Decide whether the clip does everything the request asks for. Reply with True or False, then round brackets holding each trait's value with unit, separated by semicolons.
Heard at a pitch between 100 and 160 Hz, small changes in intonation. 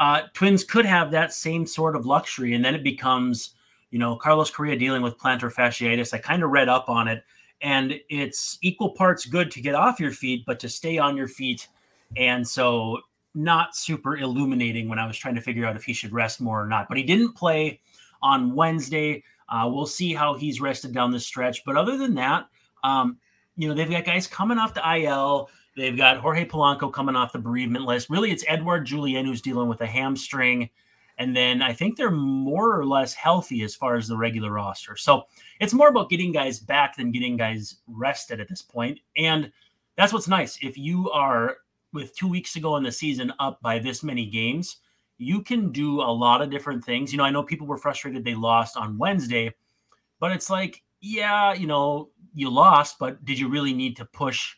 False (140 Hz; 4.8 semitones)